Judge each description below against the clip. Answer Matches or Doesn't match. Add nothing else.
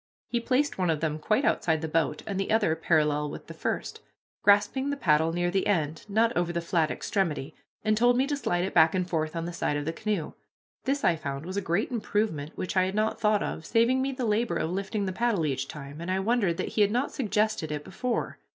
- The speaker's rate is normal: Doesn't match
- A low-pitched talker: Doesn't match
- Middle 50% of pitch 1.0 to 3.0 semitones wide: Doesn't match